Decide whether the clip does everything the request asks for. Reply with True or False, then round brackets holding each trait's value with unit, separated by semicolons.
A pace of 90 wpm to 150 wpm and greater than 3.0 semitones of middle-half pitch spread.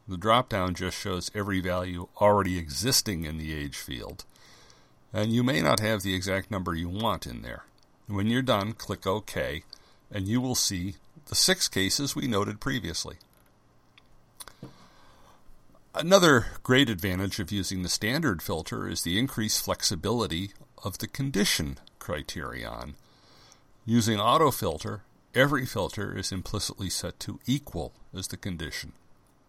True (140 wpm; 4.0 semitones)